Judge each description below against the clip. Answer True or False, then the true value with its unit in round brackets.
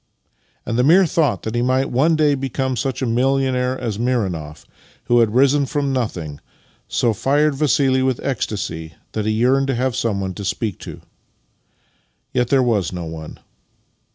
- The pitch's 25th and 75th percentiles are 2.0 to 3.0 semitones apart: False (3.9 semitones)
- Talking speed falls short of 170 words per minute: False (175 wpm)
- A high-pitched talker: False (125 Hz)